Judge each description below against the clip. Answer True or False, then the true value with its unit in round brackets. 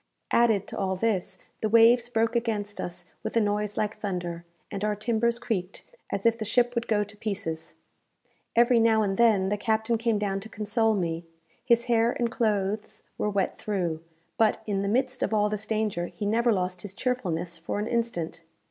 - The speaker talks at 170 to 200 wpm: True (195 wpm)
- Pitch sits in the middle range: False (210 Hz)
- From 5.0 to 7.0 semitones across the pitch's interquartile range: False (3.0 semitones)